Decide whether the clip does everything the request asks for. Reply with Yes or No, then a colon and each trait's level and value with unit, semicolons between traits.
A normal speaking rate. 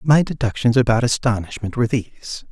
Yes: average, 145 wpm